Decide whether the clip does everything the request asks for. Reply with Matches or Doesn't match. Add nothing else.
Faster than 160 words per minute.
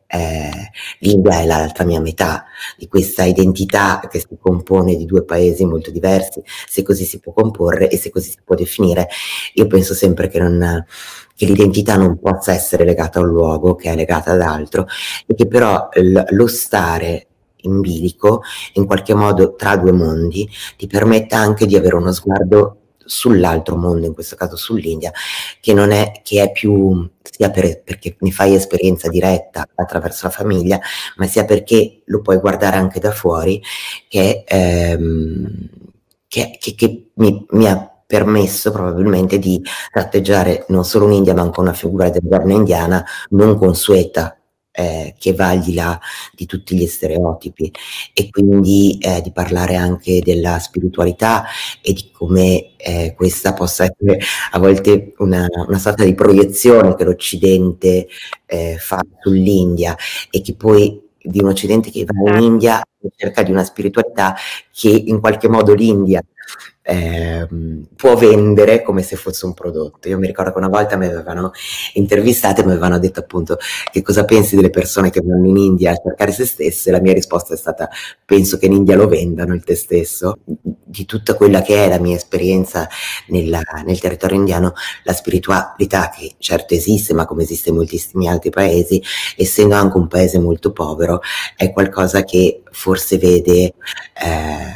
Matches